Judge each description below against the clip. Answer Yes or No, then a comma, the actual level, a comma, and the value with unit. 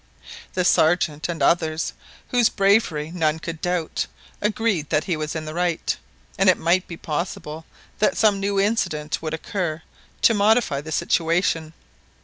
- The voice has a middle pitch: Yes, medium, 170 Hz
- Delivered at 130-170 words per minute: Yes, average, 150 wpm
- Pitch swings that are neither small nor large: Yes, average, 3.9 semitones